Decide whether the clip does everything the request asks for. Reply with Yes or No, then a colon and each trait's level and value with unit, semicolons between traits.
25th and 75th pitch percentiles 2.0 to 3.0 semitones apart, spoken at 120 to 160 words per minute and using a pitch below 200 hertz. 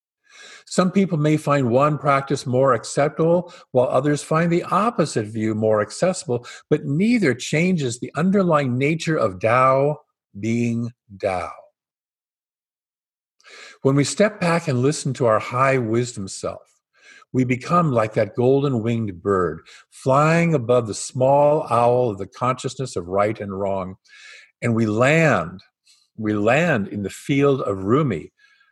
No: wide, 5.4 semitones; average, 140 wpm; low, 135 Hz